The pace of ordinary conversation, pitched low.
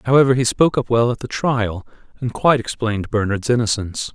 Yes: average, 190 wpm; low, 120 Hz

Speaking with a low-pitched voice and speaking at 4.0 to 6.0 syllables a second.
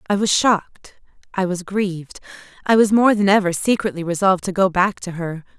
No: high, 190 Hz; 5.6 syllables/s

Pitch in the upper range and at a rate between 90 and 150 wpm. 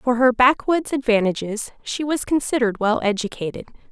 Yes: high, 240 Hz; average, 140 wpm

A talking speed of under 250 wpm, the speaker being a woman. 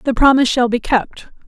Yes: fast, 205 wpm; female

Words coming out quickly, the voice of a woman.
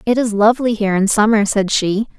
Yes: fast, 220 wpm; female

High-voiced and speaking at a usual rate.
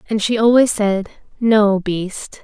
Yes: high, 210 Hz; average, 150 wpm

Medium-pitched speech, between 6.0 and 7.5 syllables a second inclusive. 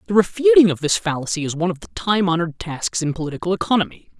Yes: medium, 175 Hz; 7.2 syllables/s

